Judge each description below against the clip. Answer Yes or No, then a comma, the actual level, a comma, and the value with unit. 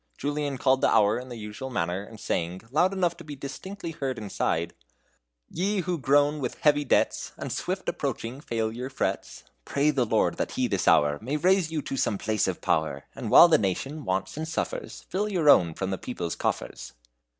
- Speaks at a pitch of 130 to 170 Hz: Yes, low, 135 Hz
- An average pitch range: No, wide, 6.8 semitones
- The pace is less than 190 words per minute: No, average, 195 wpm